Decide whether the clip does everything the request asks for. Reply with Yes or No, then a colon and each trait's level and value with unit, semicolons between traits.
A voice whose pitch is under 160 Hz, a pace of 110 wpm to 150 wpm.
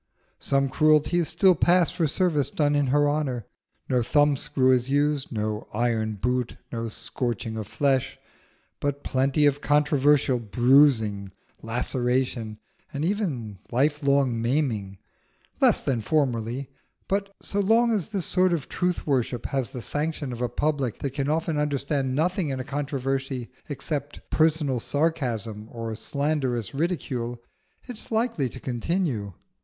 Yes: low, 135 Hz; average, 140 wpm